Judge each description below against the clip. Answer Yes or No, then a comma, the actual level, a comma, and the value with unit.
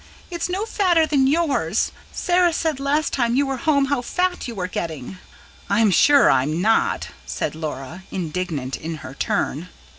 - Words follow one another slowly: No, average, 160 wpm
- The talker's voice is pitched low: No, high, 245 Hz